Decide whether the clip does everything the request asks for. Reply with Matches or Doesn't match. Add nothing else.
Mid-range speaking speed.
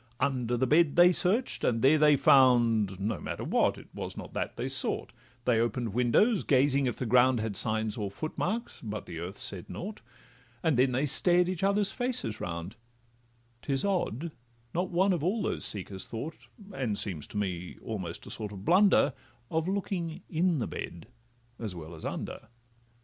Matches